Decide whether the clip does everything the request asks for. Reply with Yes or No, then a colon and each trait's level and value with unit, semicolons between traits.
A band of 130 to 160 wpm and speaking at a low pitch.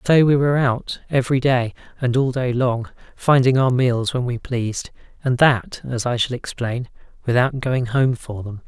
No: average, 185 wpm; low, 125 Hz